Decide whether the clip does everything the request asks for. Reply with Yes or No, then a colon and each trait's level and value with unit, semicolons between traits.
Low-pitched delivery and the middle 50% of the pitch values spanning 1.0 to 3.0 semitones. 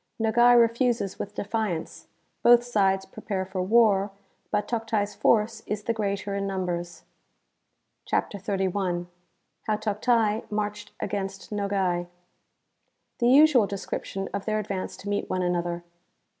No: high, 205 Hz; narrow, 2.5 semitones